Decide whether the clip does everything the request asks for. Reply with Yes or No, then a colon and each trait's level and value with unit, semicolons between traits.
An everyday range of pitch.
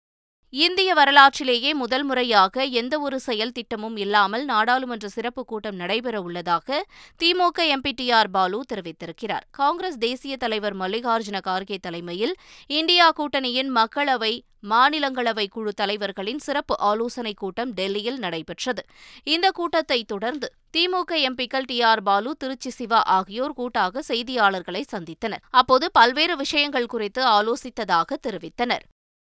Yes: average, 4.9 semitones